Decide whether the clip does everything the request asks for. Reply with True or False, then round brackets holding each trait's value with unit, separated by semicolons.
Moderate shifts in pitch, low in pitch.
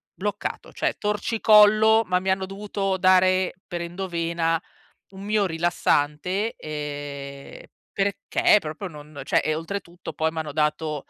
False (4.2 semitones; 180 Hz)